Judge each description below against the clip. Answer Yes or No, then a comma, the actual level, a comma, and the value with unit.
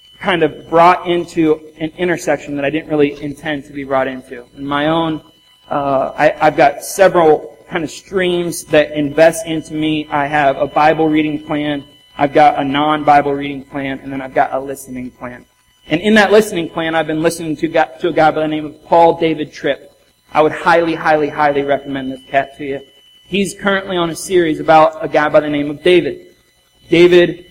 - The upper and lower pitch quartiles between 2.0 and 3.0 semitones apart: Yes, narrow, 2.4 semitones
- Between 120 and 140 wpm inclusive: No, average, 200 wpm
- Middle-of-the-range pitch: Yes, medium, 155 Hz